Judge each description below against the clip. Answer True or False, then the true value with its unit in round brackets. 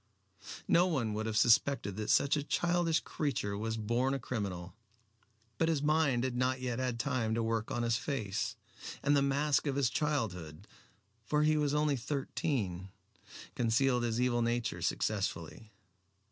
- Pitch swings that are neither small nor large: True (4.4 semitones)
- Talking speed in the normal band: True (160 wpm)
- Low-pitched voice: True (120 Hz)